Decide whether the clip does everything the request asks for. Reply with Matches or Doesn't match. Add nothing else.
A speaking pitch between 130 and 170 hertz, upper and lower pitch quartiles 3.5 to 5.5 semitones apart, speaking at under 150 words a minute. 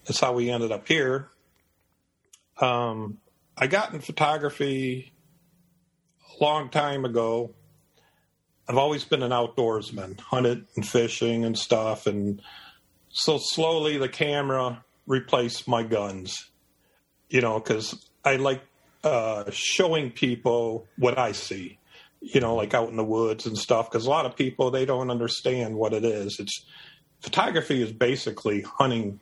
Doesn't match